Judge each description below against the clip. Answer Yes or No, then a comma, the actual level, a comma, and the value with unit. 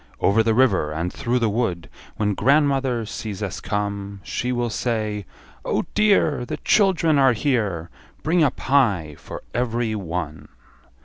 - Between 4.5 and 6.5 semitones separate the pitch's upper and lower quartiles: Yes, average, 4.8 semitones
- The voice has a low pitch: Yes, low, 115 Hz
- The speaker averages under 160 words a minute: Yes, average, 145 wpm